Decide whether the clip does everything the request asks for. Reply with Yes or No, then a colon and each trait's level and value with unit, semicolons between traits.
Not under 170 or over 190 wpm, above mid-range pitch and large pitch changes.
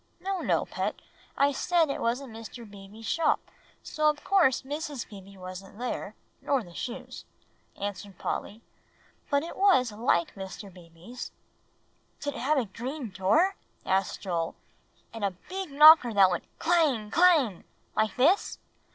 No: average, 145 wpm; high, 240 Hz; wide, 7.2 semitones